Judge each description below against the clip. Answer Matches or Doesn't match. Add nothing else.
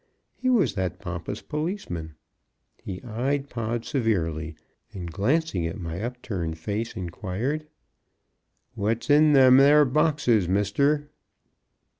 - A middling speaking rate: Doesn't match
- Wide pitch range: Matches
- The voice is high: Doesn't match